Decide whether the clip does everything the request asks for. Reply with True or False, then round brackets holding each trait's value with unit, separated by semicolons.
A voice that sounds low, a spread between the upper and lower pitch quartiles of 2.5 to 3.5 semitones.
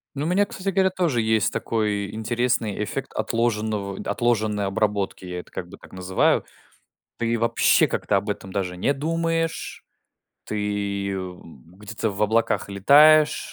False (110 Hz; 4.1 semitones)